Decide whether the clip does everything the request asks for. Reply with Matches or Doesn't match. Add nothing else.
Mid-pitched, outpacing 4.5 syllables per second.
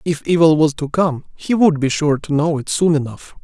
Matches